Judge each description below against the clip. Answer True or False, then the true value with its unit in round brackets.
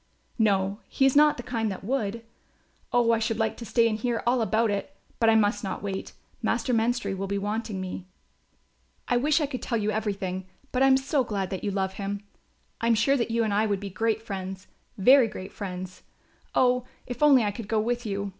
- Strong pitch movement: False (3.5 semitones)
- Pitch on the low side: False (220 Hz)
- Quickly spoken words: True (220 wpm)